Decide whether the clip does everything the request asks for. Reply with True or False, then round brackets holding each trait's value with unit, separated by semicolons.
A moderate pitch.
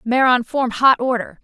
False (250 Hz)